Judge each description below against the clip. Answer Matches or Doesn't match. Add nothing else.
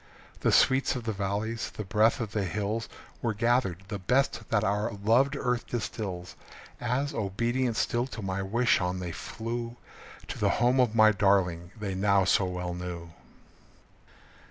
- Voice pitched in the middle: Doesn't match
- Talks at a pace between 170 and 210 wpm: Doesn't match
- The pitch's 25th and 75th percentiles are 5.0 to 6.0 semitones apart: Doesn't match